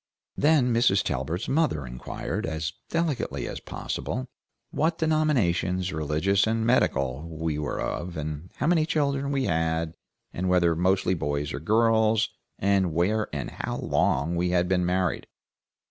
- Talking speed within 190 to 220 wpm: No, average, 140 wpm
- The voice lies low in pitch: Yes, very low, 90 Hz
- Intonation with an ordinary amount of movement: No, wide, 6.4 semitones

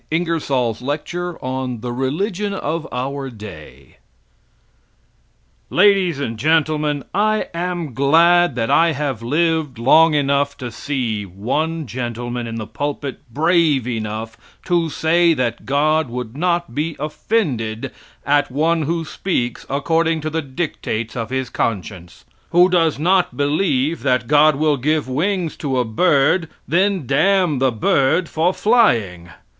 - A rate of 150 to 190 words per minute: No, slow, 135 wpm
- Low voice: No, medium, 145 Hz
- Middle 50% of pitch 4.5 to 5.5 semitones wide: Yes, average, 5.1 semitones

